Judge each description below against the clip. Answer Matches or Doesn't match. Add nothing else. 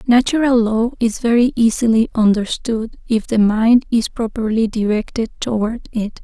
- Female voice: Matches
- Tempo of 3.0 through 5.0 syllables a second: Matches